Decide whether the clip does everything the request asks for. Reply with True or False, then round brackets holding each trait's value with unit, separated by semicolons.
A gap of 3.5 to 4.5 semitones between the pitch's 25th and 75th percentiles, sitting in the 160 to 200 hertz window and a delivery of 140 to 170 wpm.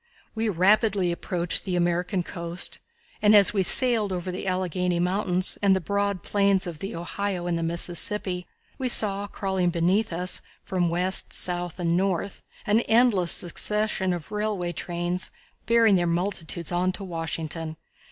False (2.6 semitones; 185 Hz; 150 wpm)